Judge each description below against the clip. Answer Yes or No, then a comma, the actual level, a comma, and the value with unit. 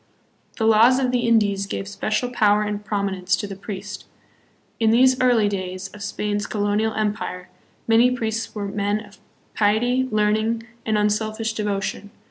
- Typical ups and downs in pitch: No, narrow, 1.7 semitones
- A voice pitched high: Yes, high, 210 Hz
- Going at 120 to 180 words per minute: Yes, average, 160 wpm